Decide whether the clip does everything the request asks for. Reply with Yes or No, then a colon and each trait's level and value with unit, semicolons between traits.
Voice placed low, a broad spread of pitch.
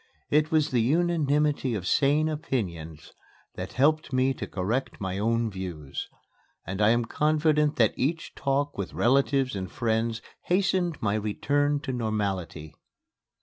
Yes: low, 130 Hz; wide, 6.2 semitones